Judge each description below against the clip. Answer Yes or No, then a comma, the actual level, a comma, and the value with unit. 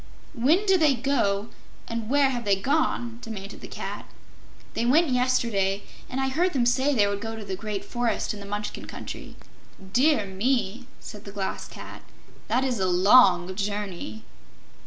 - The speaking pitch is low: No, high, 230 Hz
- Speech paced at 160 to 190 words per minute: Yes, average, 170 wpm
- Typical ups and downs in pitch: Yes, average, 4.7 semitones